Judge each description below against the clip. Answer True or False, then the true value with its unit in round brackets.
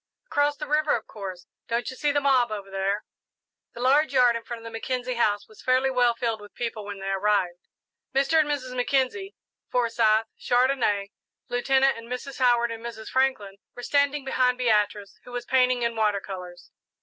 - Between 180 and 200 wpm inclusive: True (185 wpm)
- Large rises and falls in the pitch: False (3.7 semitones)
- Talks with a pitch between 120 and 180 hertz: False (240 Hz)